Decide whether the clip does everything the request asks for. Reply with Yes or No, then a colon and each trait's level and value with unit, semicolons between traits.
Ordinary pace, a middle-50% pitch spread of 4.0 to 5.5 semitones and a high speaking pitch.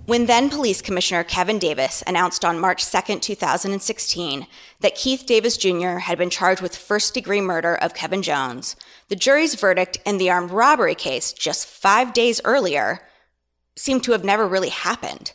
Yes: average, 165 wpm; average, 4.7 semitones; high, 195 Hz